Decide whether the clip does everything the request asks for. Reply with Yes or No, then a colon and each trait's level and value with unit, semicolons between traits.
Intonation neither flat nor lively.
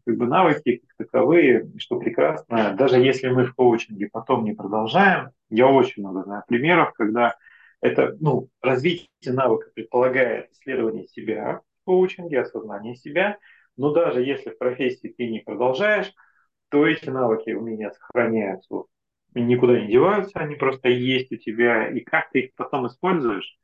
Yes: average, 4.5 semitones